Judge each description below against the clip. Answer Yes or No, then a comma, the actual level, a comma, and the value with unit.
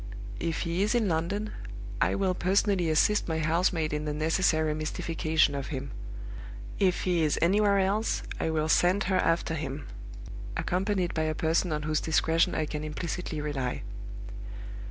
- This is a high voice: No, medium, 165 Hz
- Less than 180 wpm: Yes, average, 155 wpm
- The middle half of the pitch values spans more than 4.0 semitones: No, average, 3.1 semitones